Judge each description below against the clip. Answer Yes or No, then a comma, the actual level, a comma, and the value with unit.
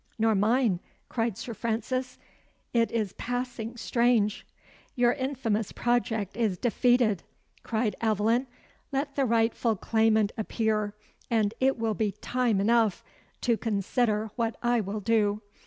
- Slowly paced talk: Yes, slow, 125 wpm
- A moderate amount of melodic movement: No, narrow, 2.2 semitones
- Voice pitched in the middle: No, high, 225 Hz